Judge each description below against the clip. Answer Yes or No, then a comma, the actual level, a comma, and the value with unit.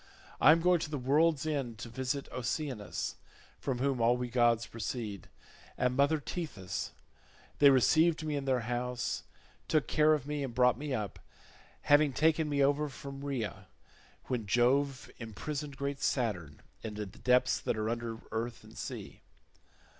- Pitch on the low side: Yes, low, 130 Hz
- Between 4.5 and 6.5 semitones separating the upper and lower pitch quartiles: No, average, 3.8 semitones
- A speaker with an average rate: Yes, average, 160 wpm